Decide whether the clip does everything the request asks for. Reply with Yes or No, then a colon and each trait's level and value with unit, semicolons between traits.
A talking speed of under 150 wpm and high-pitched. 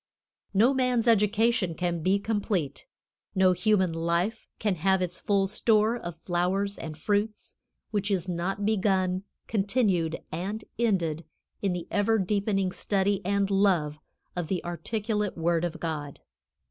Yes: slow, 135 wpm; high, 195 Hz